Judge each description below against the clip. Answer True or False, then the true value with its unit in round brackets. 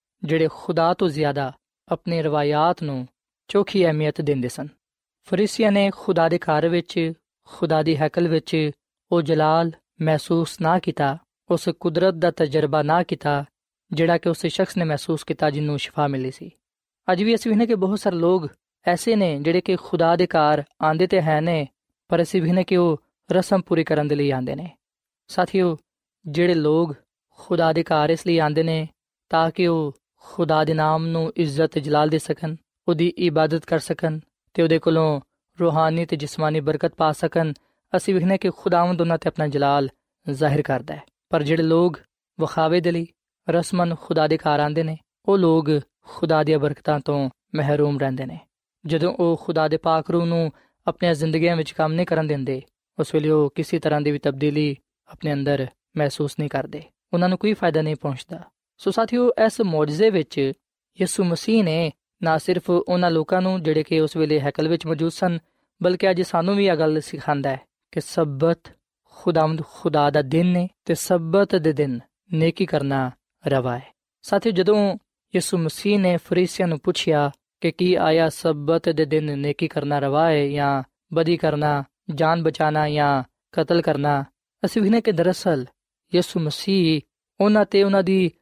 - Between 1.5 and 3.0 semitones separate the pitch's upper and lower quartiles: True (2.7 semitones)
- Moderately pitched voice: True (165 Hz)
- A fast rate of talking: True (170 wpm)